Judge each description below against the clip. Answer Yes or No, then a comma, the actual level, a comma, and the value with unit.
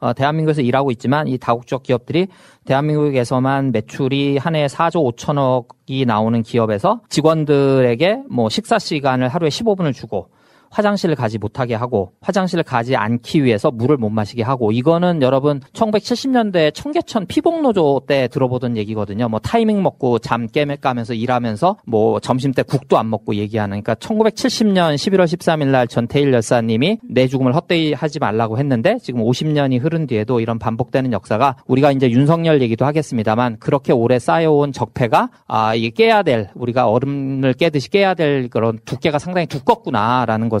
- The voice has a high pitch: No, low, 135 Hz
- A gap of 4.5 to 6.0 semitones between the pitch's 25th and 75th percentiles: Yes, average, 5.2 semitones